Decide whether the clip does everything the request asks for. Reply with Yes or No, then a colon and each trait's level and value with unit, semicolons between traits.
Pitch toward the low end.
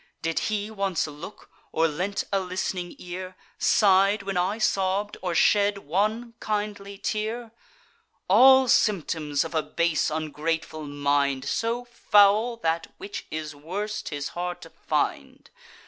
No: high, 190 Hz